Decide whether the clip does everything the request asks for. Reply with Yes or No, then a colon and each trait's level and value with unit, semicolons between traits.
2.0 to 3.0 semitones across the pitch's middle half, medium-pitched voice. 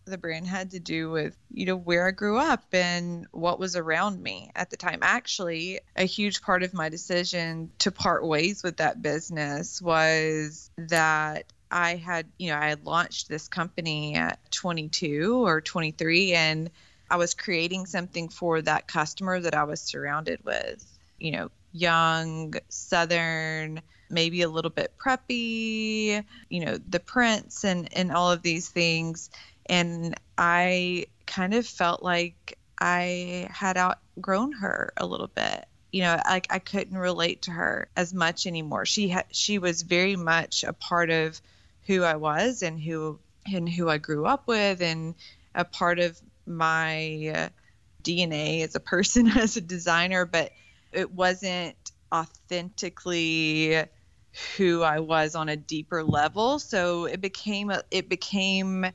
Yes: narrow, 2.5 semitones; medium, 175 Hz